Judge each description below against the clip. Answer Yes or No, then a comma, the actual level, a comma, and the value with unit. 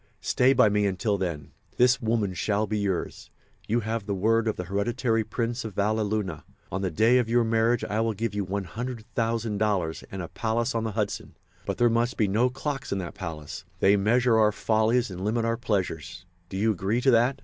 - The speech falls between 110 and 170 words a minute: No, average, 200 wpm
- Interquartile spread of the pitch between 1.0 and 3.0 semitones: Yes, average, 2.7 semitones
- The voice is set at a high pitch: No, low, 110 Hz